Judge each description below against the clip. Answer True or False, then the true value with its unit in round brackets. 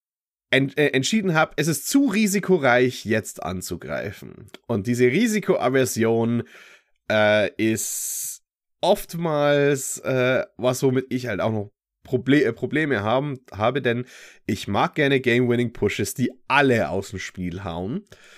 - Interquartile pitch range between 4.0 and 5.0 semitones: True (4.6 semitones)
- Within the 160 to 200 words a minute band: False (125 wpm)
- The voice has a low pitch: True (125 Hz)